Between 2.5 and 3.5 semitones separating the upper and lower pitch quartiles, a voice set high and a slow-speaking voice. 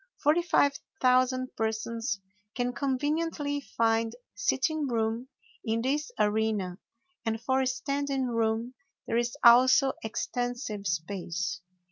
Yes: average, 3.2 semitones; high, 240 Hz; slow, 105 wpm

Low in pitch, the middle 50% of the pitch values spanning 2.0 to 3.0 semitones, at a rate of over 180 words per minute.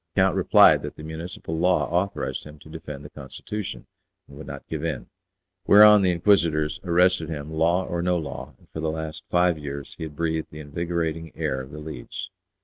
Yes: very low, 80 Hz; average, 2.7 semitones; average, 200 wpm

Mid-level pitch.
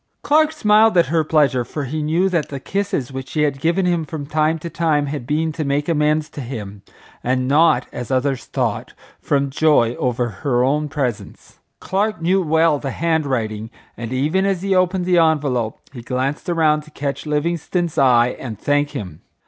Yes: medium, 150 Hz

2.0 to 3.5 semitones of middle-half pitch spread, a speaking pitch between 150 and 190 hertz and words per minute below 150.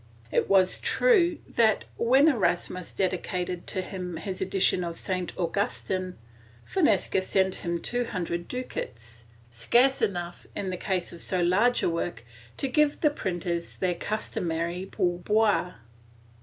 No: average, 3.9 semitones; medium, 185 Hz; average, 140 wpm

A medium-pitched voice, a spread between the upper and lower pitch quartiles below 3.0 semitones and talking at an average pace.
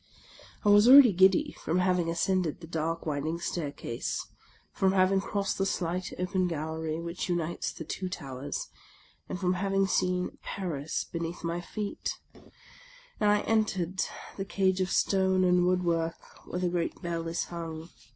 Yes: medium, 180 Hz; narrow, 2.5 semitones; average, 160 wpm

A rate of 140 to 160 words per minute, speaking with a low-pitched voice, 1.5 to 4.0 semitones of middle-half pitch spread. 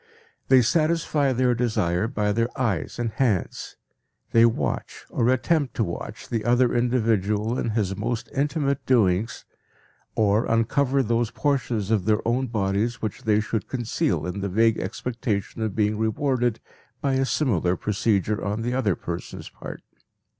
Yes: average, 150 wpm; low, 115 Hz; average, 3.3 semitones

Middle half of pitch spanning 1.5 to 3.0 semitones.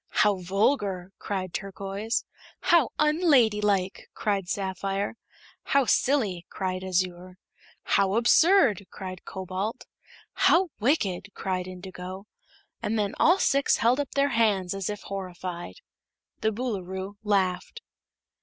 No: average, 3.6 semitones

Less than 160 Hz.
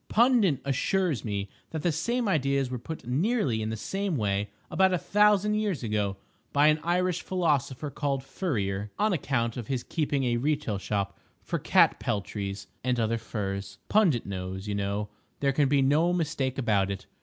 Yes: low, 135 Hz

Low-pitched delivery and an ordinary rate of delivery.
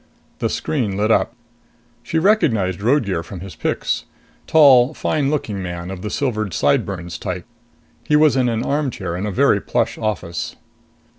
Yes: low, 110 Hz; average, 155 wpm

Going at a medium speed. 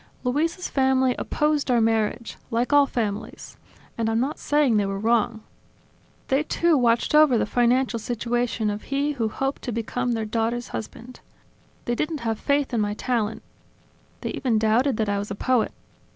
Yes: average, 170 wpm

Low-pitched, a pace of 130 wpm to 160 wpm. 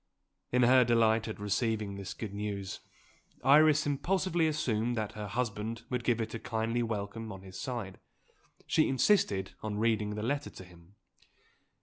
Yes: low, 115 Hz; average, 155 wpm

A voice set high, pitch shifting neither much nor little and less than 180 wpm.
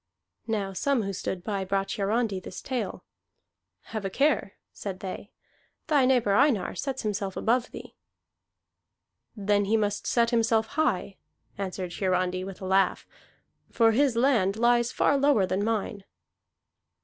Yes: high, 210 Hz; average, 3.6 semitones; average, 140 wpm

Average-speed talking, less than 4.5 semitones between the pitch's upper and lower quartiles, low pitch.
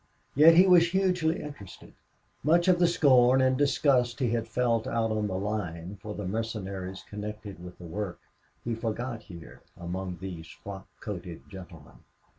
No: average, 160 wpm; wide, 5.5 semitones; low, 110 Hz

